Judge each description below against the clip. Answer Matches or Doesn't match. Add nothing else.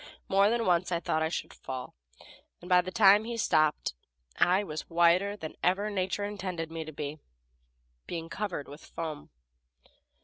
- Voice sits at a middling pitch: Matches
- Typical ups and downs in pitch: Matches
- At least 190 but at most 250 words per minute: Doesn't match